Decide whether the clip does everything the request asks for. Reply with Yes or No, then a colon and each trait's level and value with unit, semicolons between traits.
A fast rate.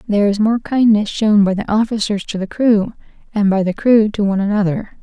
Yes: fast, 215 wpm